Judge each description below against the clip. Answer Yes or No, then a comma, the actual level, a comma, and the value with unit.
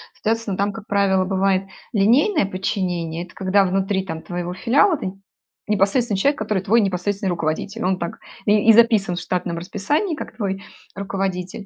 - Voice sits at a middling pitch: No, high, 195 Hz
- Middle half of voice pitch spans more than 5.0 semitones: No, narrow, 2.5 semitones